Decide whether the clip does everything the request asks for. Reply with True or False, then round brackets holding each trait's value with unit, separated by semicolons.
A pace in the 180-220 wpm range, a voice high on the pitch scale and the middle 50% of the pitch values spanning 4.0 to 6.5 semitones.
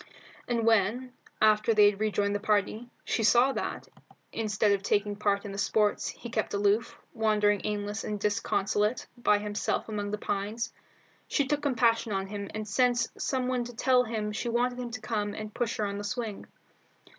False (185 wpm; 215 Hz; 2.4 semitones)